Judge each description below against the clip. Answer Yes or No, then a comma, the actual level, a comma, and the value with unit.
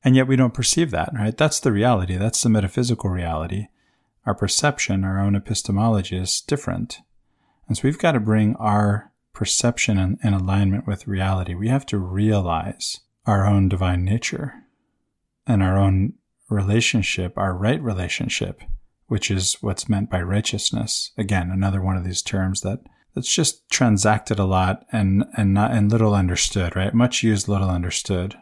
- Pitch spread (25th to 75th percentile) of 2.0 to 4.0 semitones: Yes, average, 2.9 semitones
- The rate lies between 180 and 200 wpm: No, average, 165 wpm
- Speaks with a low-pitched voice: Yes, low, 105 Hz